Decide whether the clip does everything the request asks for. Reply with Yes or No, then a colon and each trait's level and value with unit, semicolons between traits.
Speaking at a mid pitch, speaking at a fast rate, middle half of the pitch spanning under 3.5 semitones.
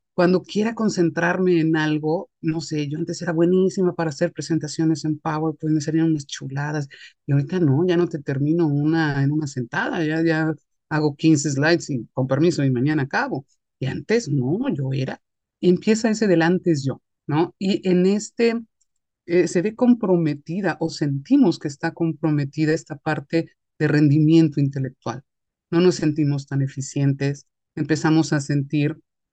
No: medium, 155 Hz; average, 165 wpm; average, 2.9 semitones